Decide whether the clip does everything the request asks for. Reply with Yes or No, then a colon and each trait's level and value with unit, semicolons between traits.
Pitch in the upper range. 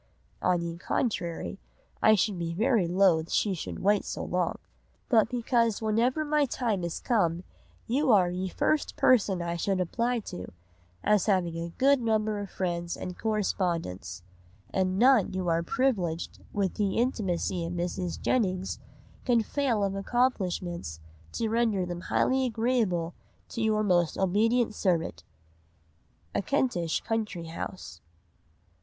Yes: high, 195 Hz